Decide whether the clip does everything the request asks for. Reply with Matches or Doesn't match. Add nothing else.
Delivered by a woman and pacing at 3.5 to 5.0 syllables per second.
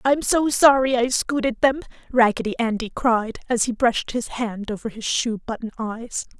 Matches